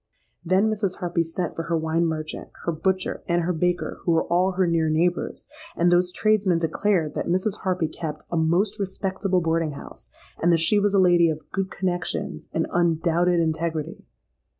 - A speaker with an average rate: Yes, average, 180 wpm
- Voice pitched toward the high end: No, medium, 175 Hz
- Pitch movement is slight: Yes, narrow, 2.3 semitones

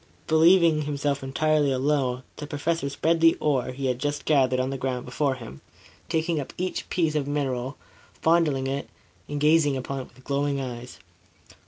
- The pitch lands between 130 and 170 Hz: Yes, medium, 140 Hz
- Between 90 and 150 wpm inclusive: No, average, 170 wpm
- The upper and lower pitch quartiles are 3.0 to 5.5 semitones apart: No, narrow, 2.6 semitones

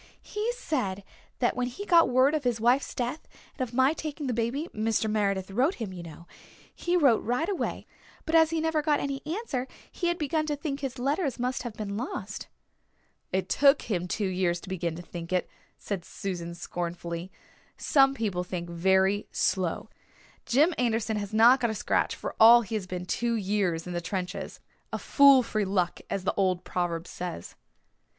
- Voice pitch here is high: Yes, high, 225 Hz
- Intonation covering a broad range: Yes, wide, 6.9 semitones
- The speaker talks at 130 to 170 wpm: No, average, 190 wpm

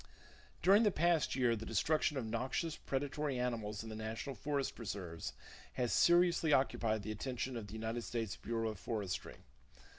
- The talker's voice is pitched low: Yes, low, 120 Hz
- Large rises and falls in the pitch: No, average, 4.6 semitones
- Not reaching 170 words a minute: Yes, average, 160 wpm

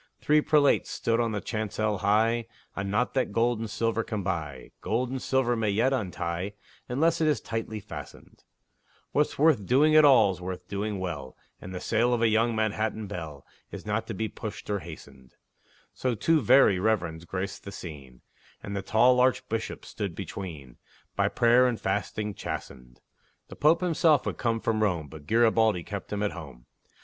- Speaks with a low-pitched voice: Yes, low, 110 Hz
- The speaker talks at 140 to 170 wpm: No, average, 180 wpm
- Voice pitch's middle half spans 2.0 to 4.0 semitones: No, average, 4.4 semitones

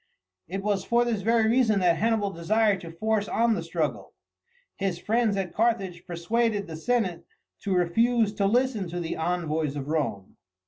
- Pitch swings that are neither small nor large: Yes, average, 4.8 semitones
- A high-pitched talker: Yes, high, 200 Hz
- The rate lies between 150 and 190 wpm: Yes, average, 170 wpm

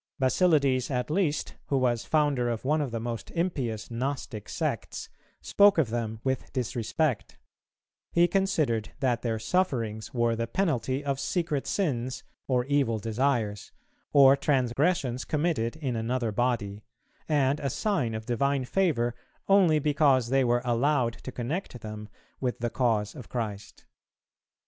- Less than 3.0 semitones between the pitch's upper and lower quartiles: No, average, 4.0 semitones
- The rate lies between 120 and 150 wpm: Yes, average, 140 wpm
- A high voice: No, low, 130 Hz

